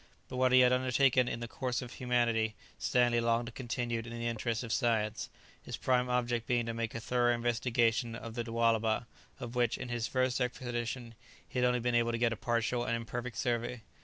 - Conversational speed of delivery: No, fast, 210 wpm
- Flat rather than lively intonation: Yes, narrow, 1.2 semitones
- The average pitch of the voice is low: Yes, low, 120 Hz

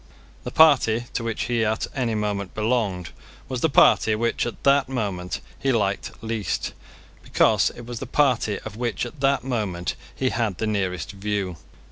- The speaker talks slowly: No, average, 170 wpm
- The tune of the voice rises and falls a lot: No, average, 3.5 semitones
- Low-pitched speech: Yes, low, 110 Hz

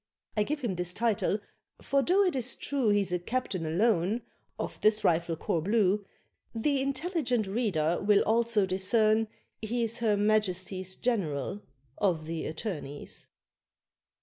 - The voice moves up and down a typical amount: Yes, average, 4.6 semitones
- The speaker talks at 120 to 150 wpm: Yes, slow, 135 wpm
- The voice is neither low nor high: No, high, 210 Hz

